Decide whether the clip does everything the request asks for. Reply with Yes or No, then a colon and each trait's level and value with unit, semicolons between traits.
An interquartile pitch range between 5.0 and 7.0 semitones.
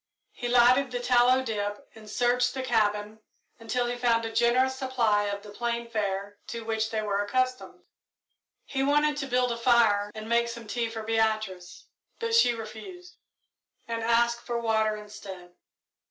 No: narrow, 2.4 semitones